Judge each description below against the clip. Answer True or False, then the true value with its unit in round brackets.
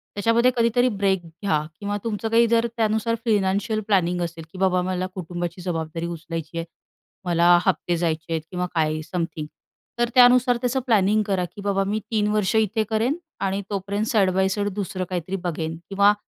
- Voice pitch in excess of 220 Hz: False (195 Hz)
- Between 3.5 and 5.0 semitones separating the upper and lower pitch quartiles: True (3.8 semitones)